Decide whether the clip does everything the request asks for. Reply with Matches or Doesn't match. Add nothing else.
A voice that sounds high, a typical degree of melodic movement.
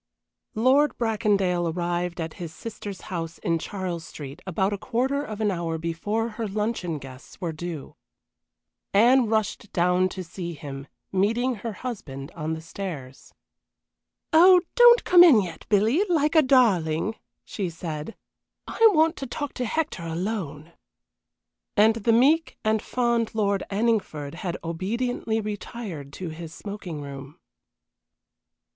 Doesn't match